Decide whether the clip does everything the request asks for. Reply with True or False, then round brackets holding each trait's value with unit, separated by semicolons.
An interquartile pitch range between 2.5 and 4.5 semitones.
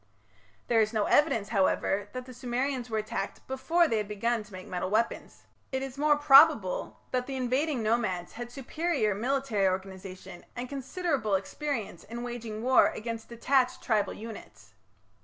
True (4.2 semitones)